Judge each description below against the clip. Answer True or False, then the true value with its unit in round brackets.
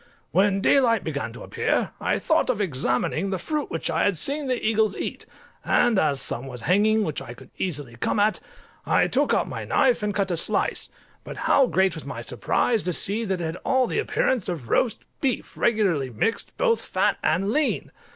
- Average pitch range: False (6.5 semitones)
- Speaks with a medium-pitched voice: False (195 Hz)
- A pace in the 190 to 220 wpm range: True (200 wpm)